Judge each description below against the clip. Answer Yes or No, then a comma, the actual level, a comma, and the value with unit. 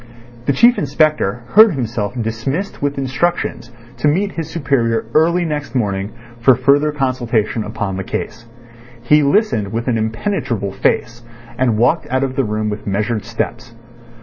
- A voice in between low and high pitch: No, low, 125 Hz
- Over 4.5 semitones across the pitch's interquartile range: Yes, average, 5.0 semitones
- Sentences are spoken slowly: No, average, 150 wpm